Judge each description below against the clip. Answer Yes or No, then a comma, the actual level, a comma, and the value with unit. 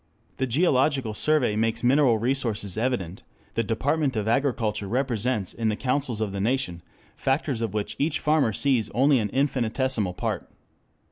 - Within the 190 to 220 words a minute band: No, average, 150 wpm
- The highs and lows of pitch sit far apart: No, average, 3.9 semitones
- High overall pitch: No, low, 120 Hz